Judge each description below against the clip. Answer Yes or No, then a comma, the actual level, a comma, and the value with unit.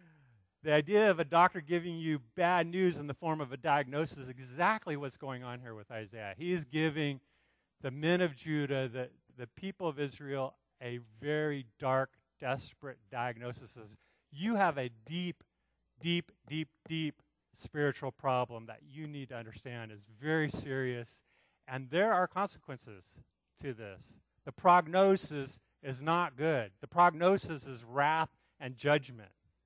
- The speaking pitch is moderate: Yes, medium, 145 Hz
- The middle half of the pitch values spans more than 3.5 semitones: Yes, average, 4.9 semitones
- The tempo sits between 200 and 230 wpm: No, average, 150 wpm